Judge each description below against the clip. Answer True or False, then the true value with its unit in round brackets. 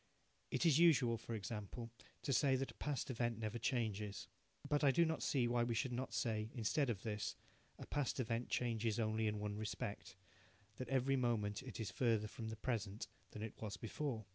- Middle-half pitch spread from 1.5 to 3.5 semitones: True (3.2 semitones)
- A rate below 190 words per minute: False (195 wpm)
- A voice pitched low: True (115 Hz)